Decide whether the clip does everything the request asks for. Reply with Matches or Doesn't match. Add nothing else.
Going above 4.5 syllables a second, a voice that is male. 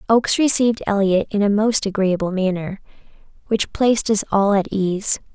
Doesn't match